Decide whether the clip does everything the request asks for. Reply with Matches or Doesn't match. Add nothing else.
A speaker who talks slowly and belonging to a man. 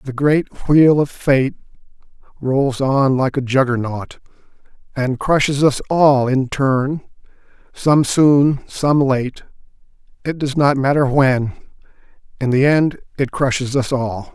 Matches